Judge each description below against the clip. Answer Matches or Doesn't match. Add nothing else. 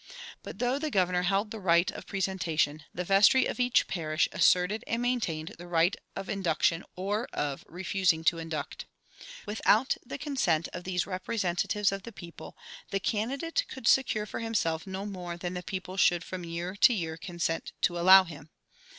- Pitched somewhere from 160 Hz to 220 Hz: Matches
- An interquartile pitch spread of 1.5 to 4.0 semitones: Matches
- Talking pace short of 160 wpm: Doesn't match